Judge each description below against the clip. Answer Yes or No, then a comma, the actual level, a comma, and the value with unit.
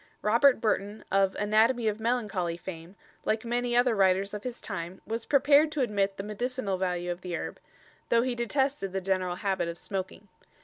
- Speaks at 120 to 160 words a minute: No, average, 180 wpm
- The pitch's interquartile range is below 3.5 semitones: No, average, 4.2 semitones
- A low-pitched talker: No, high, 210 Hz